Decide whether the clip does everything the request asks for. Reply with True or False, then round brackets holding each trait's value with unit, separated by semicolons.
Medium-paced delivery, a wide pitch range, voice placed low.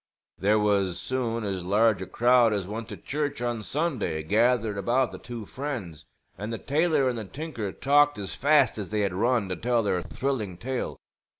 False (190 wpm; 4.4 semitones; 115 Hz)